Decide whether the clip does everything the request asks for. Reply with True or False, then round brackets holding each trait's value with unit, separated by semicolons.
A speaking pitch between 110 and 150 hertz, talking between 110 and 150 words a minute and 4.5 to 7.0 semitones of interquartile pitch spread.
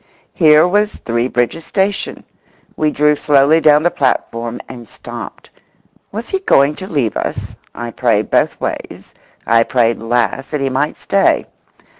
True (140 Hz; 145 wpm; 5.2 semitones)